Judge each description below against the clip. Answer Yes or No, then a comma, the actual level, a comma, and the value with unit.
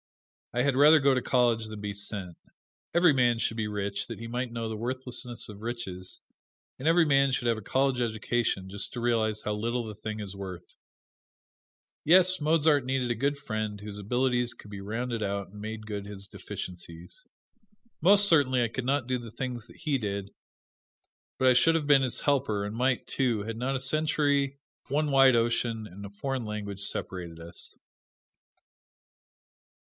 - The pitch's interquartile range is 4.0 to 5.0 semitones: Yes, average, 4.4 semitones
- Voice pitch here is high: No, low, 120 Hz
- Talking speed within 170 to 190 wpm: Yes, average, 180 wpm